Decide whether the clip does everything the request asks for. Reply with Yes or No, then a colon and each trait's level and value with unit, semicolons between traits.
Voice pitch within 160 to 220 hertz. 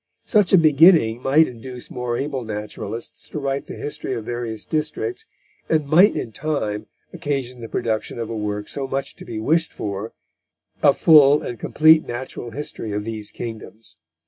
No: low, 125 Hz